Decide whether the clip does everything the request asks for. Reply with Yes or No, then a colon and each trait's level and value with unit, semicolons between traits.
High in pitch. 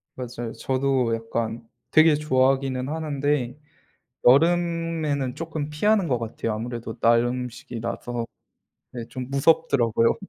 No: low, 130 Hz